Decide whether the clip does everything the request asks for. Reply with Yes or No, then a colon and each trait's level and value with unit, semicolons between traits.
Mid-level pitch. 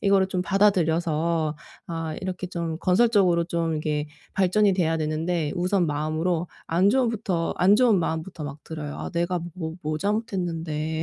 Yes: medium, 170 Hz